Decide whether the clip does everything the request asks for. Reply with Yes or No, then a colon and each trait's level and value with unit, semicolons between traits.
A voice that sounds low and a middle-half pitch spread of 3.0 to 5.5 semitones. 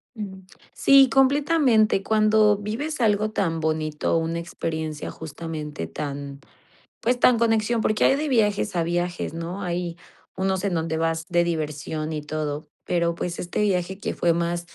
No: medium, 175 Hz; average, 4.9 semitones